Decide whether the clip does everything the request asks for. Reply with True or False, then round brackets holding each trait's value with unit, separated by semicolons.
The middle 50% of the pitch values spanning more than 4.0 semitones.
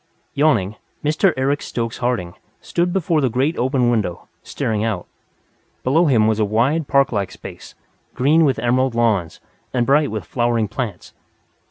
True (4.5 semitones)